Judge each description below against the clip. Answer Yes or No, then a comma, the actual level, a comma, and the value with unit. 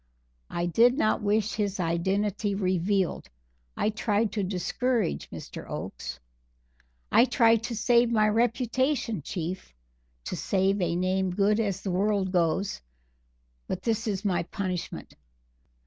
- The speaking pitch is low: No, high, 200 Hz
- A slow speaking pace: Yes, slow, 130 wpm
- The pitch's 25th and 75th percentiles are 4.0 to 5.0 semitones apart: No, average, 3.4 semitones